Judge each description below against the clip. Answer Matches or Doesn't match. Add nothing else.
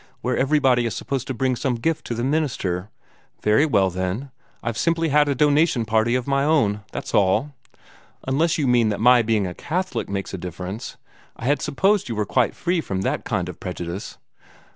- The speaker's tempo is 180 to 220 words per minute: Matches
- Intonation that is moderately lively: Doesn't match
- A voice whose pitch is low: Matches